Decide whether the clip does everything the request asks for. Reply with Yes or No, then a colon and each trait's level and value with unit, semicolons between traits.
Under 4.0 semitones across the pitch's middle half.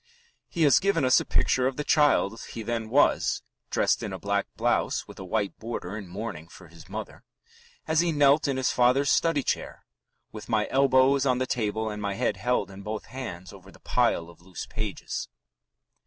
No: average, 5.1 semitones